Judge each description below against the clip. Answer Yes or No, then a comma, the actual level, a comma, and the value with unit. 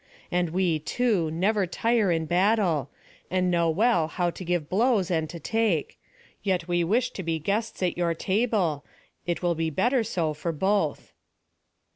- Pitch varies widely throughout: No, average, 4.0 semitones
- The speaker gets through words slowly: No, average, 165 wpm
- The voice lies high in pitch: No, medium, 180 Hz